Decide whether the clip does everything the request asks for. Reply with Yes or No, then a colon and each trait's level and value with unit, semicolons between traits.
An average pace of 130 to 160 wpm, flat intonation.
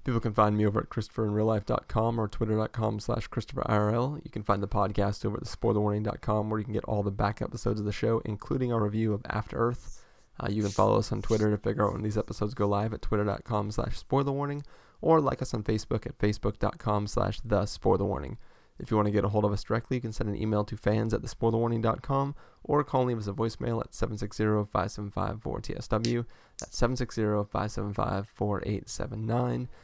No: average, 190 wpm; narrow, 2.3 semitones